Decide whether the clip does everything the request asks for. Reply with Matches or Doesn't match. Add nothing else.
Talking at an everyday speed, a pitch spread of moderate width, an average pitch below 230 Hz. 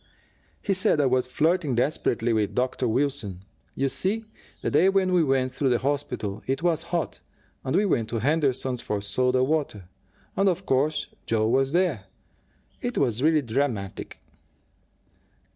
Matches